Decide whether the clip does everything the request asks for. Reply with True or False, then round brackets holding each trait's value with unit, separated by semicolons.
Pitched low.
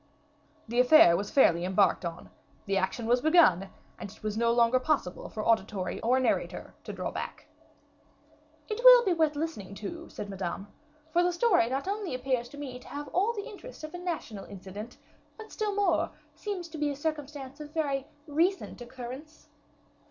False (270 Hz)